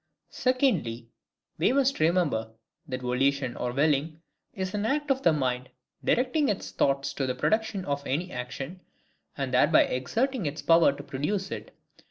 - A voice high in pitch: No, medium, 155 Hz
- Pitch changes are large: Yes, wide, 8.0 semitones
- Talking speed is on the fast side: No, average, 155 wpm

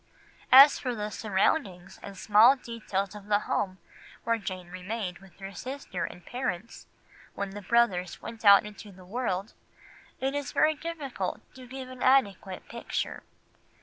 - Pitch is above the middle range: Yes, high, 210 Hz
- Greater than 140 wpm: Yes, average, 150 wpm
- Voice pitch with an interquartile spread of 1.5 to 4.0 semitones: No, average, 4.8 semitones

